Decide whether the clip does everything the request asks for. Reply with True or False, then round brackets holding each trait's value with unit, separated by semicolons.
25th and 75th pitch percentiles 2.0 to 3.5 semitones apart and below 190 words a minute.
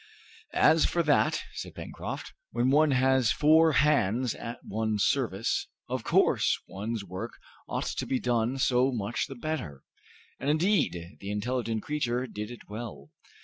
False (4.7 semitones; 145 wpm)